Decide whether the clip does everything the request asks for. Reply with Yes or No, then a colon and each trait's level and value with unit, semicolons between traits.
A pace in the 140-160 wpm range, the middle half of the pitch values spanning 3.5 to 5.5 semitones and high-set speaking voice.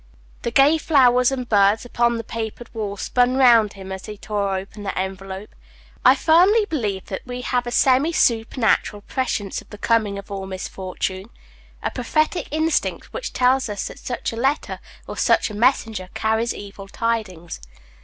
No: average, 170 wpm; average, 4.1 semitones; high, 225 Hz